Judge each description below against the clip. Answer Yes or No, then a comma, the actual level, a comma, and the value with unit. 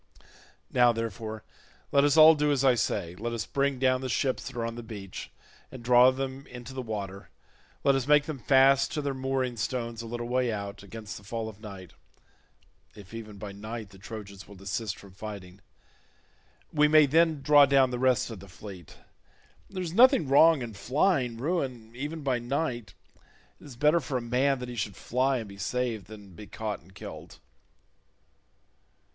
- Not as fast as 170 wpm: No, average, 185 wpm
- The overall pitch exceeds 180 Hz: No, low, 120 Hz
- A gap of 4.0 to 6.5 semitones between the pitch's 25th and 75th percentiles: Yes, average, 4.4 semitones